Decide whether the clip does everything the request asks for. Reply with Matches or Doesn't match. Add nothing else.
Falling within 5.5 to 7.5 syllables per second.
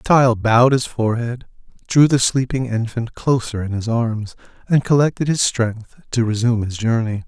Doesn't match